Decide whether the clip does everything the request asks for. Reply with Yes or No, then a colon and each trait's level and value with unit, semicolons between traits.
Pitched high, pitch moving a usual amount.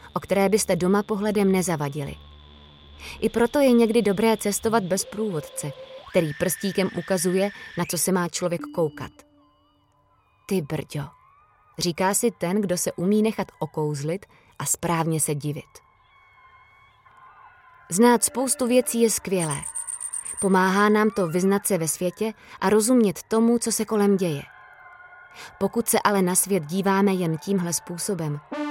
Yes: high, 195 Hz; average, 4.8 semitones